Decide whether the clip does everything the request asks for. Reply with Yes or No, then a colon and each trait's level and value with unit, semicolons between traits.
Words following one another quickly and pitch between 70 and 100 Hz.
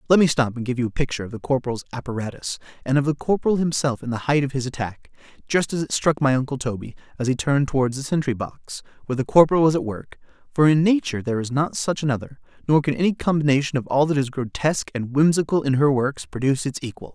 No: fast, 230 wpm; low, 135 Hz